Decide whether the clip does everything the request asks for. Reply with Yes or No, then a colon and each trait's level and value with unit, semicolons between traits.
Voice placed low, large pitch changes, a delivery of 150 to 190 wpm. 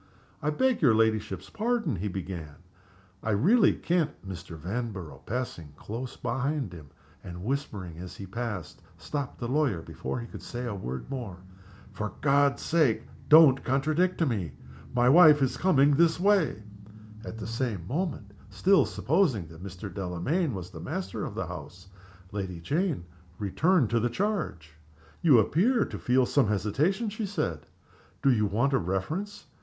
Yes: low, 120 Hz; wide, 8.3 semitones; average, 160 wpm